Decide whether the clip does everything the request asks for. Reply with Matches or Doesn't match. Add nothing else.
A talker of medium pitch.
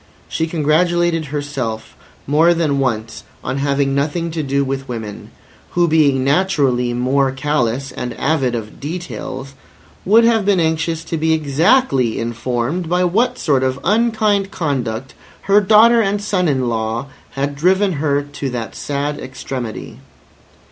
Matches